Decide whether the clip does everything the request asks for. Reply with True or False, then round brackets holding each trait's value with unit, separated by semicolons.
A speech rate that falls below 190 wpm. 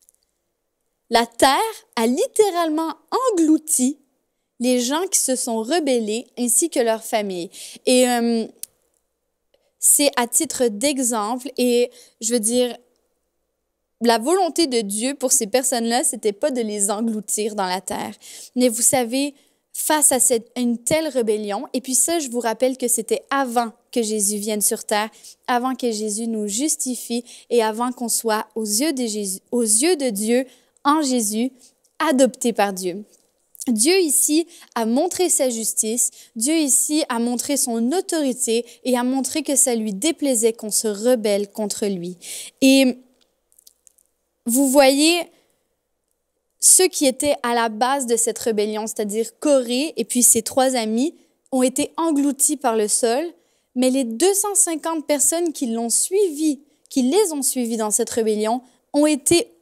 True (150 wpm)